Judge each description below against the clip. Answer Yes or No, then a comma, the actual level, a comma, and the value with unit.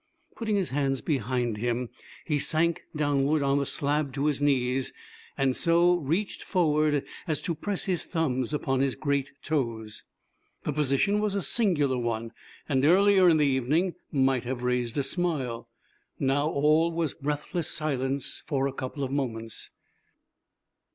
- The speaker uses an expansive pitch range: No, average, 3.6 semitones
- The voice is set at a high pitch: No, medium, 140 Hz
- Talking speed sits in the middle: Yes, average, 150 wpm